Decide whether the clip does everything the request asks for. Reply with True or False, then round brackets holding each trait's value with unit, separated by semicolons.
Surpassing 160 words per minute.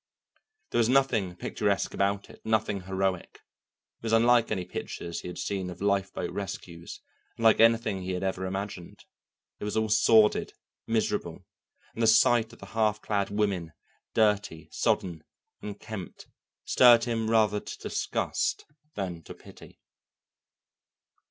False (140 wpm)